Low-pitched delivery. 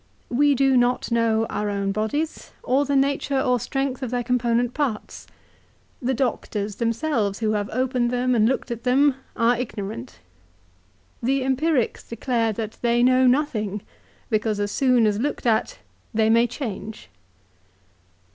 No: high, 240 Hz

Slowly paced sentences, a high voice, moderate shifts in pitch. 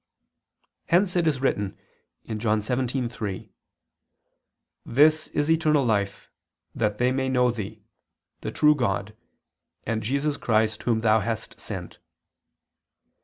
No: slow, 115 wpm; low, 120 Hz; average, 4.7 semitones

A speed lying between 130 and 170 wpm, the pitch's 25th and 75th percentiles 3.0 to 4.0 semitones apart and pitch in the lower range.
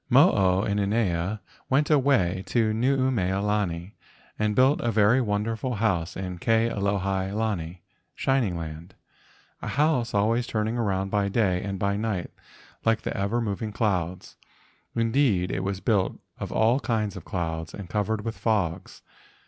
Yes: average, 150 wpm; average, 3.3 semitones; low, 105 Hz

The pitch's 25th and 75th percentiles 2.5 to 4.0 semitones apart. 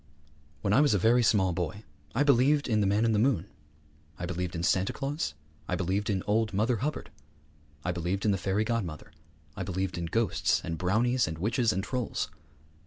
No: average, 4.4 semitones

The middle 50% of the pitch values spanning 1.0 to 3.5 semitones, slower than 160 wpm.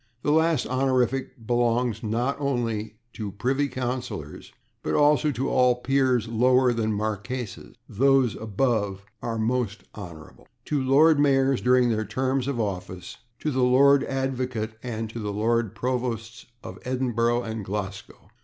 Yes: average, 3.2 semitones; average, 145 wpm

